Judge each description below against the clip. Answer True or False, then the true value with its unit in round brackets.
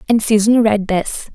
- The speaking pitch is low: False (215 Hz)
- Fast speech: False (180 wpm)